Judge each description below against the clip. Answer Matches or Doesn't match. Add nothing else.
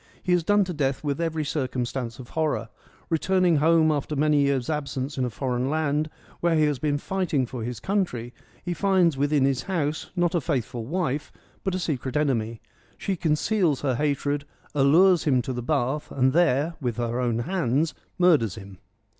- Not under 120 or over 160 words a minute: Doesn't match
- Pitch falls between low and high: Matches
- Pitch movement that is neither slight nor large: Matches